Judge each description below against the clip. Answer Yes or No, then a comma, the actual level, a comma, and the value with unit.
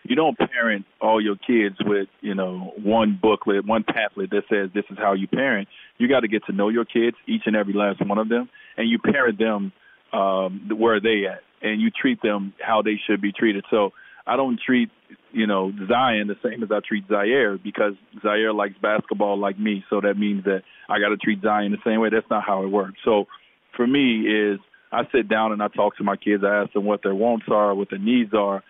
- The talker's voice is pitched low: Yes, low, 105 Hz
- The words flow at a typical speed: No, fast, 235 wpm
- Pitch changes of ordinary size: No, narrow, 1.7 semitones